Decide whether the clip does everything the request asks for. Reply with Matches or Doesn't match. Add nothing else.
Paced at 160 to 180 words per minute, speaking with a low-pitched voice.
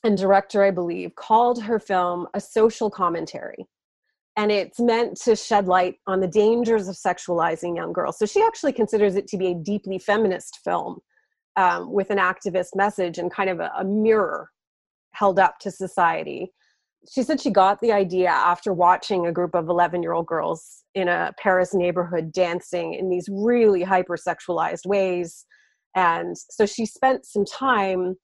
Doesn't match